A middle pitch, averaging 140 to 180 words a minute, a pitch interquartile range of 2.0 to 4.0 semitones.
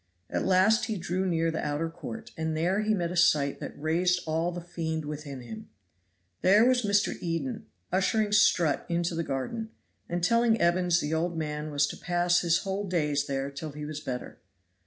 No: medium, 170 Hz; average, 190 wpm; average, 3.7 semitones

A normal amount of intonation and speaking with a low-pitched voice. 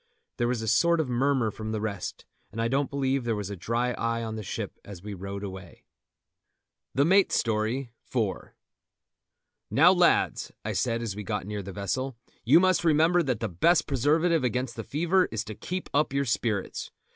Yes: average, 4.9 semitones; low, 120 Hz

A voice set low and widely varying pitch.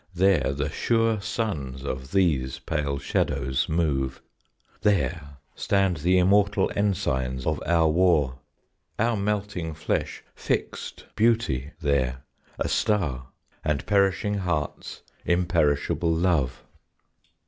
Yes: very low, 80 Hz; wide, 5.9 semitones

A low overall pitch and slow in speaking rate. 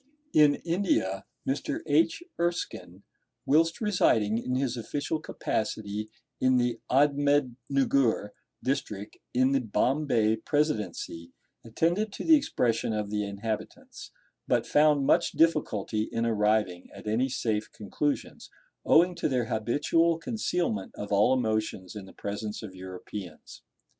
Yes: low, 120 Hz; slow, 125 wpm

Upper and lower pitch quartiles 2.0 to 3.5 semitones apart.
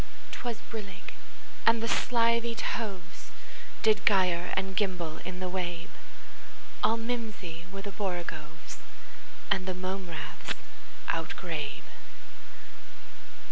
No: average, 4.0 semitones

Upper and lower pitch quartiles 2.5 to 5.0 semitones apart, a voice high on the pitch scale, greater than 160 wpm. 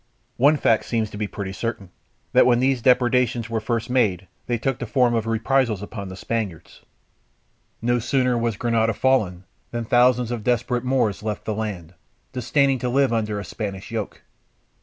No: average, 2.8 semitones; low, 115 Hz; average, 175 wpm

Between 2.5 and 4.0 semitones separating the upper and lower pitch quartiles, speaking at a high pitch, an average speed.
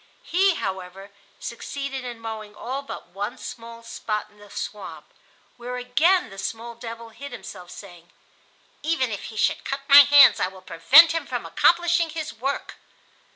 No: wide, 5.4 semitones; high, 235 Hz; average, 160 wpm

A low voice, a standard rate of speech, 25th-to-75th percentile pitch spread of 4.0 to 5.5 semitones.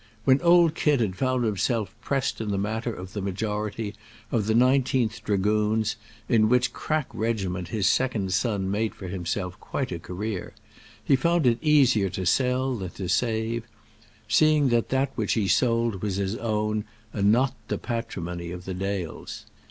Yes: low, 110 Hz; average, 165 wpm; average, 4.3 semitones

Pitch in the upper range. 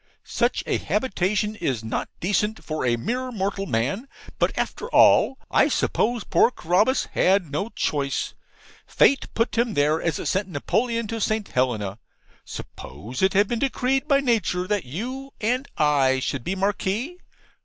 Yes: high, 200 Hz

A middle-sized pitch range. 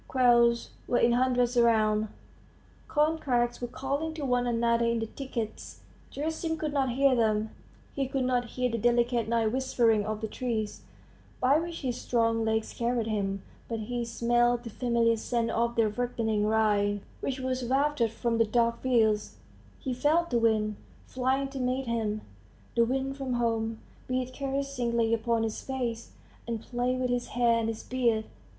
No: narrow, 2.2 semitones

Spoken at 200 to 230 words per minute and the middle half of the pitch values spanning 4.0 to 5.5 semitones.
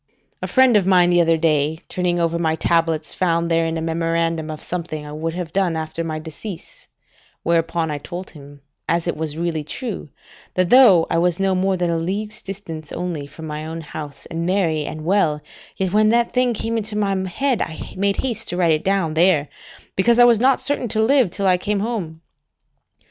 No: fast, 205 wpm; average, 3.6 semitones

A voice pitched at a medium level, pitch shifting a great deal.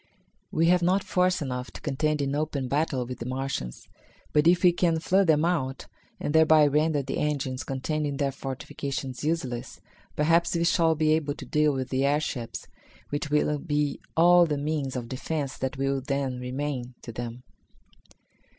No: medium, 145 Hz; average, 3.2 semitones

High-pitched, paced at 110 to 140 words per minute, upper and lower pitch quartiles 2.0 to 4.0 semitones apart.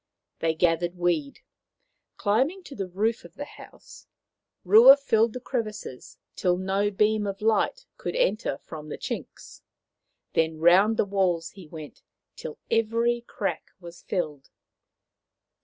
No: high, 195 Hz; slow, 135 wpm; average, 4.7 semitones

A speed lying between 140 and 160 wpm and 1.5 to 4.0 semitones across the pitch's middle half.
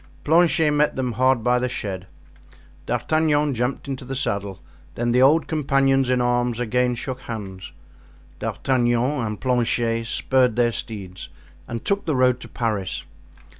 Yes: average, 145 wpm; average, 2.8 semitones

